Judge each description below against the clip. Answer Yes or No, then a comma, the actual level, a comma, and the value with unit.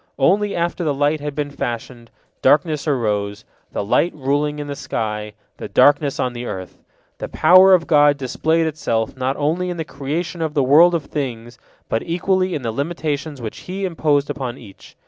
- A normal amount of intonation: Yes, average, 4.7 semitones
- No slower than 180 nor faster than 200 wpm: Yes, average, 185 wpm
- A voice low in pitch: No, medium, 145 Hz